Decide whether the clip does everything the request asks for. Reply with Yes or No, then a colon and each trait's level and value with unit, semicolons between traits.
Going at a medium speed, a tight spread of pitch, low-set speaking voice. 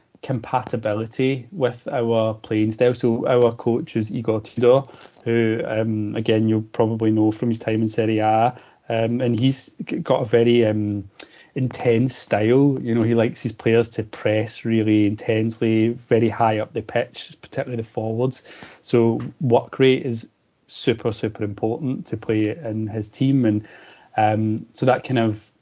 Yes: average, 160 wpm; narrow, 1.9 semitones; low, 115 Hz